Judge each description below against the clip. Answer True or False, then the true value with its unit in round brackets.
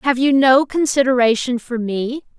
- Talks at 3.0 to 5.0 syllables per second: True (4.6 syllables/s)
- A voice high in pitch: True (255 Hz)